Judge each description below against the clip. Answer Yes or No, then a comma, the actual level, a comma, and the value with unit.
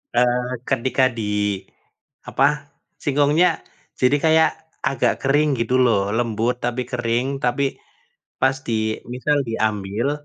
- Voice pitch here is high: No, low, 125 Hz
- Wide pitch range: No, average, 3.4 semitones